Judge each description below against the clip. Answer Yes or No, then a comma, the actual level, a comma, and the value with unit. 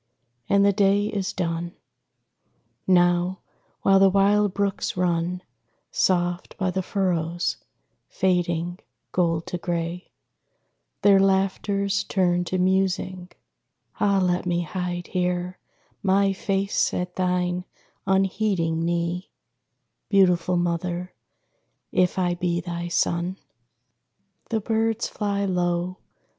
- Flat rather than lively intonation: Yes, narrow, 1.9 semitones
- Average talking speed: No, slow, 105 wpm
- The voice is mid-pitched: Yes, medium, 180 Hz